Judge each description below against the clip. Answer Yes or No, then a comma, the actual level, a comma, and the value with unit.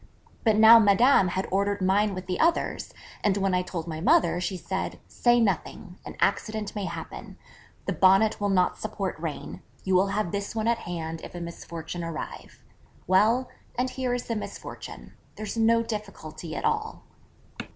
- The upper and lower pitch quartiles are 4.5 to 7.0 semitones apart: No, average, 3.4 semitones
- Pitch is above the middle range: Yes, high, 200 Hz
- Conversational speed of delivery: Yes, average, 170 wpm